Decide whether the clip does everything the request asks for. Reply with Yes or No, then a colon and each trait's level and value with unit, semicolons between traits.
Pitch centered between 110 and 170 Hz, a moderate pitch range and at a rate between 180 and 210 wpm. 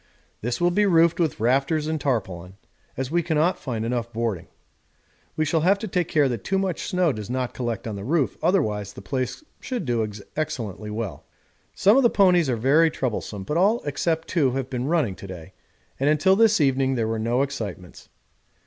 No: low, 135 Hz; wide, 6.8 semitones; average, 195 wpm